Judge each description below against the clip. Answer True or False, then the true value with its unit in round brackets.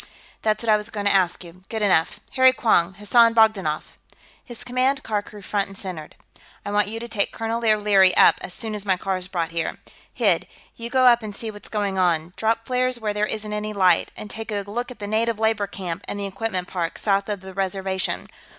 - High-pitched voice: True (205 Hz)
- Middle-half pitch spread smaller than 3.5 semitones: True (2.8 semitones)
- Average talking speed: False (225 wpm)